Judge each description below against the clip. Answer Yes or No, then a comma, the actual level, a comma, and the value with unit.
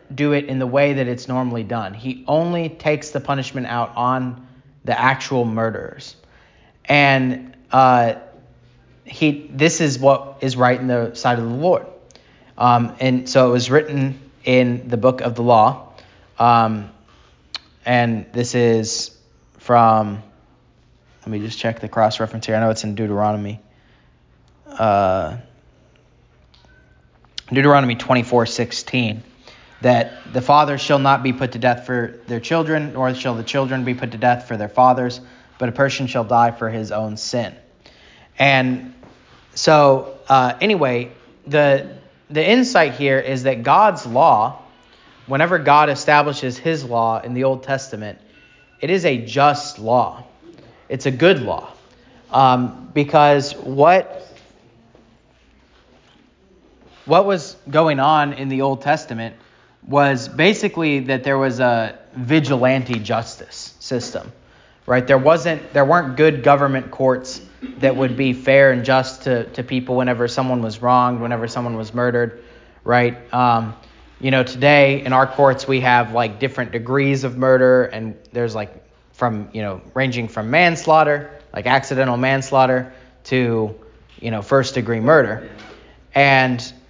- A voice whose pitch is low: Yes, low, 130 Hz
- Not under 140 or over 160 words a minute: Yes, average, 145 wpm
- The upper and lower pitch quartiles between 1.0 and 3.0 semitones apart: Yes, narrow, 2.6 semitones